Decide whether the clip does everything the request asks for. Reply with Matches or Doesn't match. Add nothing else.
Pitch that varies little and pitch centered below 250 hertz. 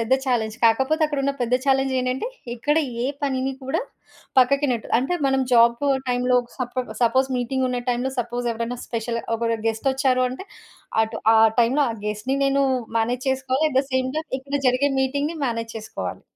Doesn't match